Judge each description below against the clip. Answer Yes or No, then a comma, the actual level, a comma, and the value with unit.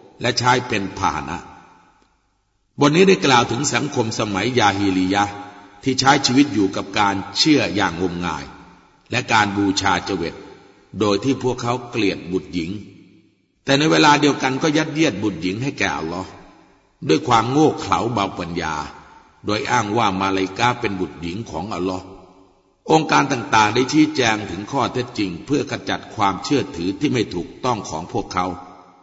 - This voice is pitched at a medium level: No, low, 100 Hz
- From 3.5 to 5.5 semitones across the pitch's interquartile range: Yes, average, 5.2 semitones